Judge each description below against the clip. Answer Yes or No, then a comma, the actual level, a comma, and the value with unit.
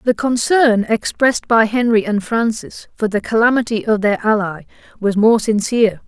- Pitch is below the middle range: No, high, 220 Hz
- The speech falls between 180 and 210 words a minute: No, average, 160 wpm